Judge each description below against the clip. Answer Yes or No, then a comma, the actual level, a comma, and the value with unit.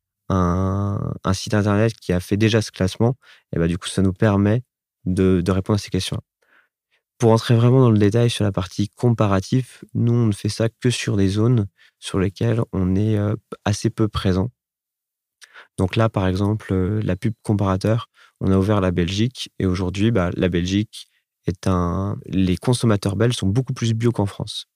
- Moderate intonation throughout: Yes, average, 3.2 semitones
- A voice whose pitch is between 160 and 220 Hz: No, low, 105 Hz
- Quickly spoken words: No, average, 185 wpm